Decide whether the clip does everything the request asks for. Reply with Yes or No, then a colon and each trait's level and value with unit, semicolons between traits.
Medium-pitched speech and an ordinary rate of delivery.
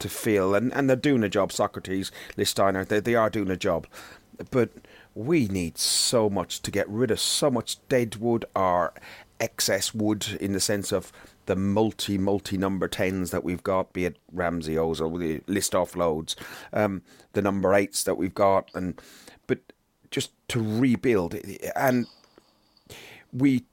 No: low, 100 Hz; average, 165 wpm